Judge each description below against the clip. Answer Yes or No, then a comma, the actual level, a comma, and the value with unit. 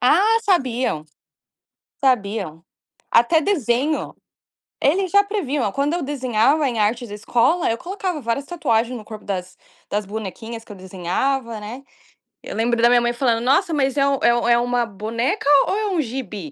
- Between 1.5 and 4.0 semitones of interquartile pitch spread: No, average, 4.7 semitones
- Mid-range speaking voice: No, high, 245 Hz